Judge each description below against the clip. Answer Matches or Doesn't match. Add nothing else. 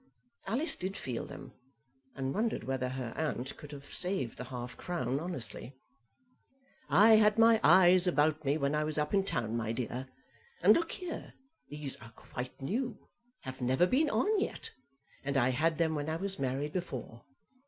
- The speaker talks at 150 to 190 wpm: Matches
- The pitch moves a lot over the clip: Matches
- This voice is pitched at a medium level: Matches